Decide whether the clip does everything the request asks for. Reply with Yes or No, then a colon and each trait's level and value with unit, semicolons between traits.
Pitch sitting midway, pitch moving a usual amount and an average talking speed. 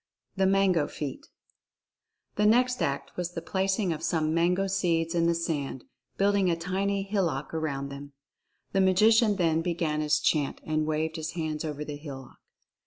Yes: medium, 165 Hz; average, 3.9 semitones; average, 165 wpm